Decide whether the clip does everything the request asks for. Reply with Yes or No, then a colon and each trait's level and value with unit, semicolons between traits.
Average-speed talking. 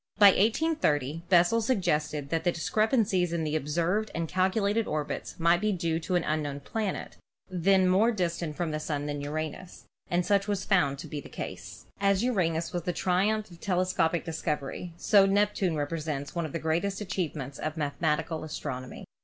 Yes: average, 170 wpm